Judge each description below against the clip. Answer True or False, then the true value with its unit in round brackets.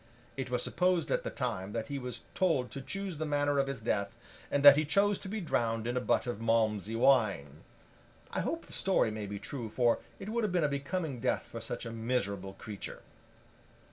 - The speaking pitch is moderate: False (125 Hz)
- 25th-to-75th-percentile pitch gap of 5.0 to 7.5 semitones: True (5.6 semitones)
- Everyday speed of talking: False (215 wpm)